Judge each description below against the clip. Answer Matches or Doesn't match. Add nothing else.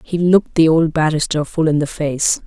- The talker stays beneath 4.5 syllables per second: Doesn't match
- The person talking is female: Matches